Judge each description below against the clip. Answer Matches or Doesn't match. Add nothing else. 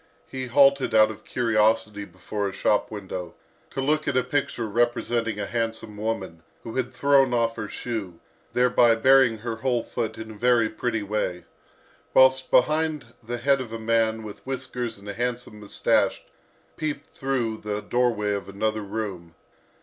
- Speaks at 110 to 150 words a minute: Doesn't match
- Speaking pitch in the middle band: Doesn't match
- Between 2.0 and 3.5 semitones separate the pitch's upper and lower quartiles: Matches